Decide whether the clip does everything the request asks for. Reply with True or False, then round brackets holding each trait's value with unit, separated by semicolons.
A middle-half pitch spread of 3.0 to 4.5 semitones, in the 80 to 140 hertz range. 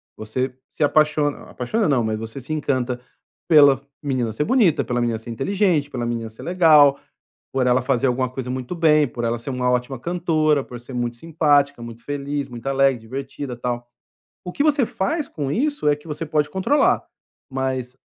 True (3.9 semitones; 135 Hz)